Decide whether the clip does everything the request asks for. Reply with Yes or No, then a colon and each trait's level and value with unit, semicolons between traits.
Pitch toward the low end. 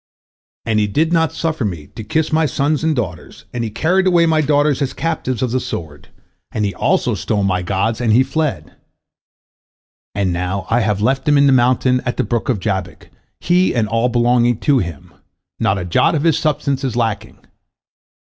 Yes: low, 120 Hz